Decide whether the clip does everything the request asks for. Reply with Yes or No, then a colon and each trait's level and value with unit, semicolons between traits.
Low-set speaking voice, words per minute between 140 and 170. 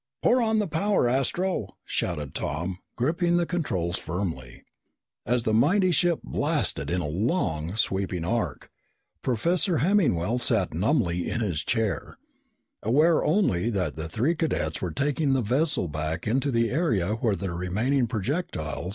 Yes: low, 115 Hz; average, 145 wpm